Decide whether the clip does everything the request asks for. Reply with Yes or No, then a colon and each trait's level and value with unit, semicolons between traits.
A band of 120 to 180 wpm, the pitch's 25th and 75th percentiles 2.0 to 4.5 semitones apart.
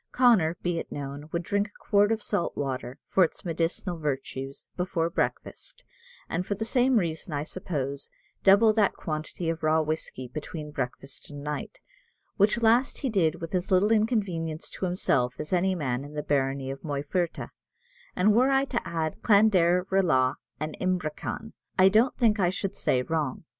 No: average, 170 wpm; average, 5.3 semitones